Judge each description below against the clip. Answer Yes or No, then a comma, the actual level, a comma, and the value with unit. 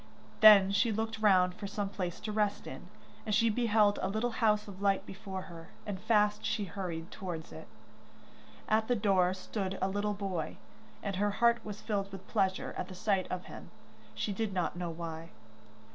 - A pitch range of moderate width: No, narrow, 2.3 semitones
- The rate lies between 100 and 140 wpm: No, average, 190 wpm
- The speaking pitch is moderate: No, high, 200 Hz